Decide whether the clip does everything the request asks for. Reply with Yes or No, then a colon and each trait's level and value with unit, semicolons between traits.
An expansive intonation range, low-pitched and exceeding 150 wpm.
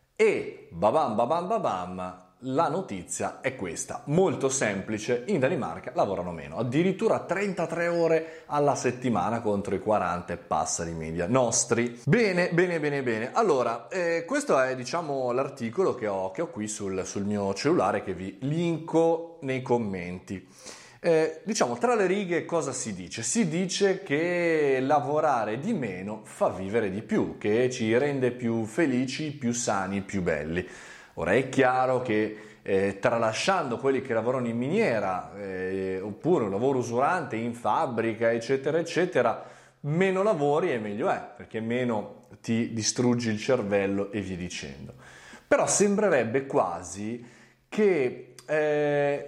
No: wide, 7.1 semitones; low, 130 Hz; average, 140 wpm